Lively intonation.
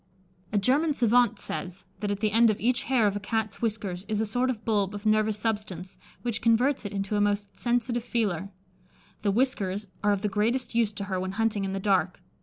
No: narrow, 2.6 semitones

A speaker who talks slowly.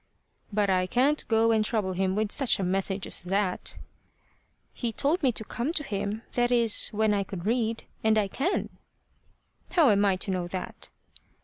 No: average, 185 wpm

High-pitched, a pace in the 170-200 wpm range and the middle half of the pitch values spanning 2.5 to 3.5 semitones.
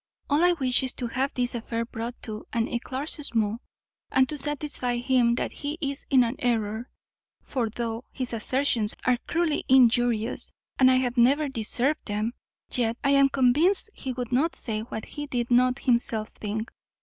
Yes: high, 245 Hz; average, 175 wpm; average, 2.9 semitones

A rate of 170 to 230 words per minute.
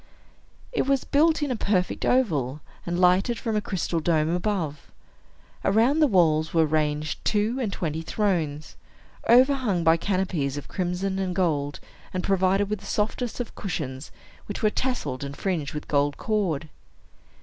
No: average, 155 wpm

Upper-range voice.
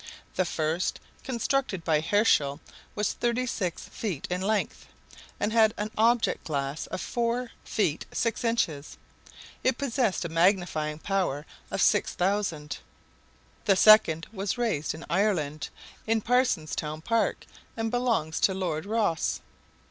Yes: high, 195 Hz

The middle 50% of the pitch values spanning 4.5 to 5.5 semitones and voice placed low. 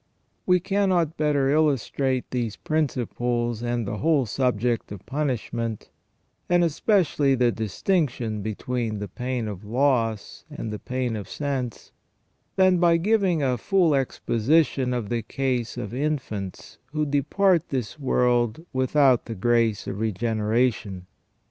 Yes: average, 4.9 semitones; low, 125 Hz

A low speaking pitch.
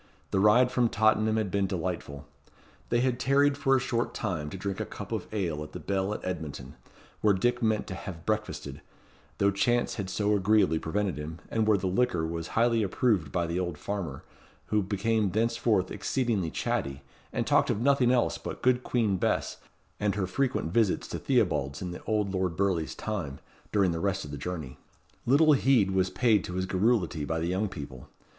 Yes: low, 100 Hz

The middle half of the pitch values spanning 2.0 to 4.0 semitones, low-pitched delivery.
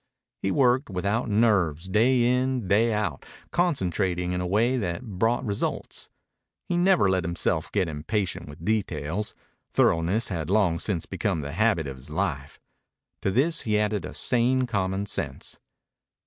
No: average, 4.8 semitones; low, 100 Hz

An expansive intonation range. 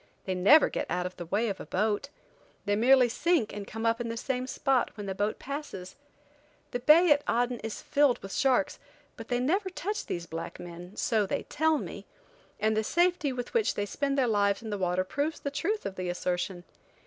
Yes: wide, 6.3 semitones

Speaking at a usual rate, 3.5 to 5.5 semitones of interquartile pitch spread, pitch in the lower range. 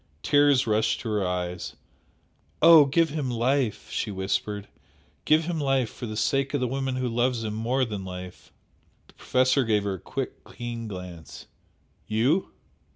Yes: average, 160 wpm; average, 4.5 semitones; low, 120 Hz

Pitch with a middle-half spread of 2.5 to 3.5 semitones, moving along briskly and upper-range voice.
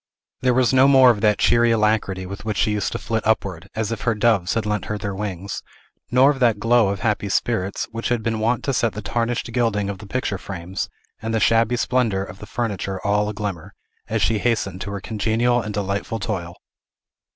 No: average, 2.8 semitones; fast, 220 wpm; low, 105 Hz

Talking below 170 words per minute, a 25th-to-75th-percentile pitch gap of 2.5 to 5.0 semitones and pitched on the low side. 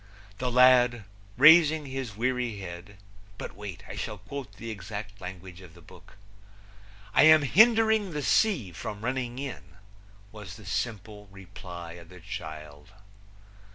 No: average, 140 wpm; wide, 5.6 semitones; low, 105 Hz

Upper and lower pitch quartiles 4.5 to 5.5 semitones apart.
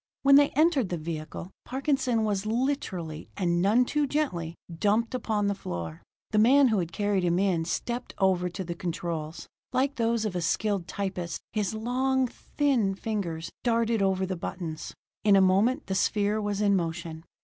Yes: average, 5.2 semitones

